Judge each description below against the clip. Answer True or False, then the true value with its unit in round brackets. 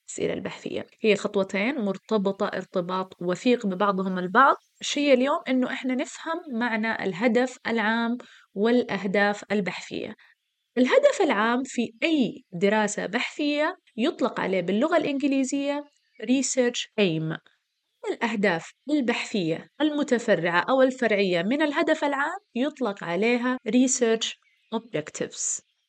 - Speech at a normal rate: True (100 wpm)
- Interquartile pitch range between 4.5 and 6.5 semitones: True (5.2 semitones)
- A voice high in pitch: True (240 Hz)